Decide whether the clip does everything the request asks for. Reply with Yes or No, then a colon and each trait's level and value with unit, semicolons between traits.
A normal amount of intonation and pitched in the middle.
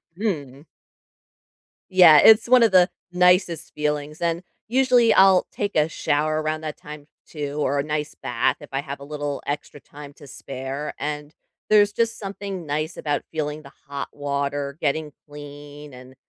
Yes: average, 3.9 semitones; medium, 150 Hz